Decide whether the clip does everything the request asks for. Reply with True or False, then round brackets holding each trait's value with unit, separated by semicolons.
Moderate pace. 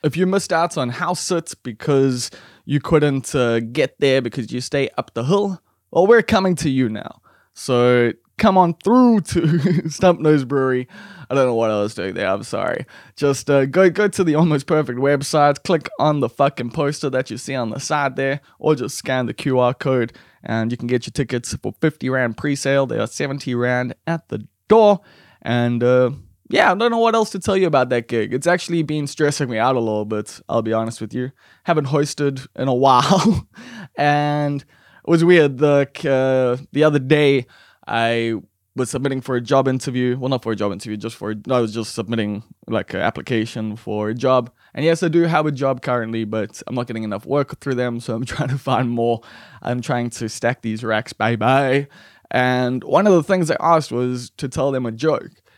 False (215 wpm)